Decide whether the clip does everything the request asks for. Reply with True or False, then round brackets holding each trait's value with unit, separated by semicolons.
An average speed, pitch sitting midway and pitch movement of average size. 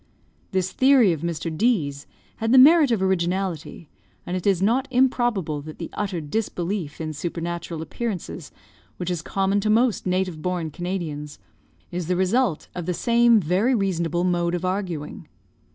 True (160 wpm; 180 Hz; 4.1 semitones)